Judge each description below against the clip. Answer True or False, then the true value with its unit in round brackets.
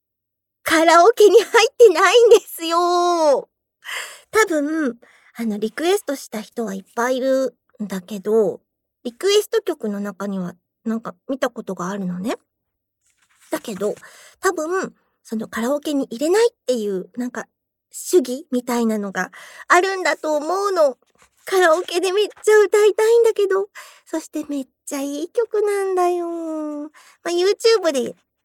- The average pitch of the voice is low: False (305 Hz)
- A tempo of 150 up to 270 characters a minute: False (295 characters per minute)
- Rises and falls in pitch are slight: False (8.7 semitones)